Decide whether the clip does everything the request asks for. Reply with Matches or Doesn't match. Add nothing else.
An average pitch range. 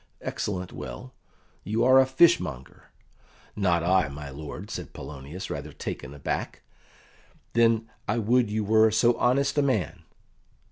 Doesn't match